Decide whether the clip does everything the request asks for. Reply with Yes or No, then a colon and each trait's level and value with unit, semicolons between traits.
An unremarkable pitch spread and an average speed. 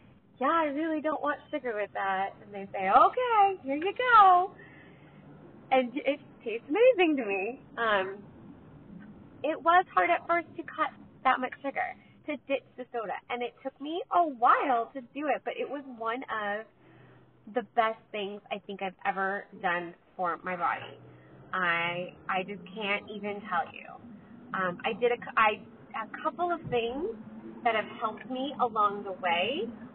No: wide, 6.7 semitones; average, 170 wpm